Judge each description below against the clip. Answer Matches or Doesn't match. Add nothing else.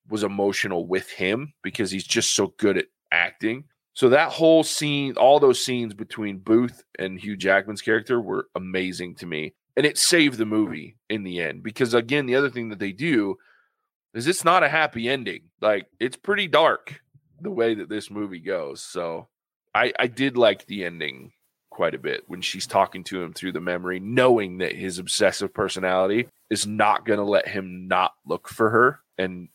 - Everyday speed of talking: Matches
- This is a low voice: Matches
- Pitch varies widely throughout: Matches